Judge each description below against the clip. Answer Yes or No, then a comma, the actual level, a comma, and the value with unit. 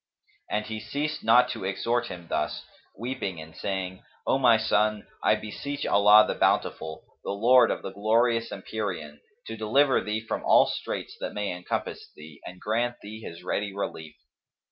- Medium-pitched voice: No, low, 105 Hz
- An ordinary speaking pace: Yes, average, 165 wpm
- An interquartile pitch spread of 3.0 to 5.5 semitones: Yes, average, 3.8 semitones